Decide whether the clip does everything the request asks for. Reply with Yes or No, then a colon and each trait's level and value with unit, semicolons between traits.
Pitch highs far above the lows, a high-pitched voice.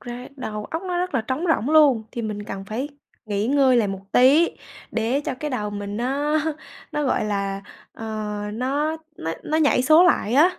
Yes: wide, 5.9 semitones; very high, 255 Hz